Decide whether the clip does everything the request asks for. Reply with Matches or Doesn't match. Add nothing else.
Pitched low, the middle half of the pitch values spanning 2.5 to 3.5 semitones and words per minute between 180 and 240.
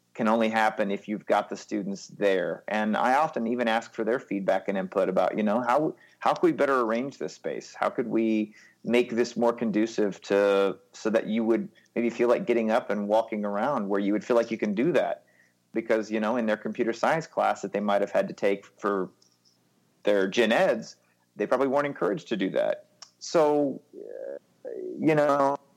Matches